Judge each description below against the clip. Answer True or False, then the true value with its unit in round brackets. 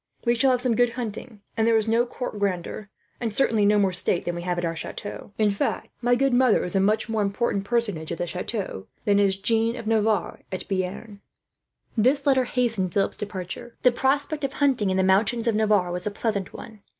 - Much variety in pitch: False (3.6 semitones)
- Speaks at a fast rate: True (210 wpm)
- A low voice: False (215 Hz)